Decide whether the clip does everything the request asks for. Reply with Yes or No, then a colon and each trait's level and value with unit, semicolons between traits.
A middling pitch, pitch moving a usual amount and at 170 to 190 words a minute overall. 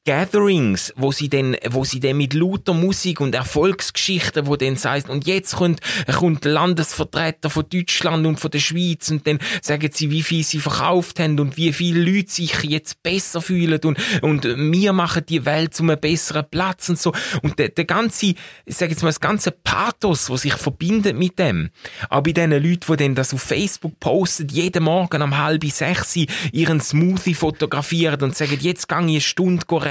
Yes: medium, 160 Hz; average, 3.0 semitones; average, 185 wpm